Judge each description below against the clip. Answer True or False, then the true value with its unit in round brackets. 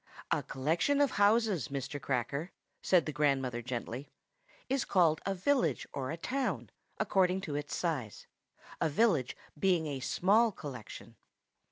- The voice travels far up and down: True (6.4 semitones)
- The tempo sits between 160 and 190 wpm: False (140 wpm)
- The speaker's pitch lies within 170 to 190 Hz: False (160 Hz)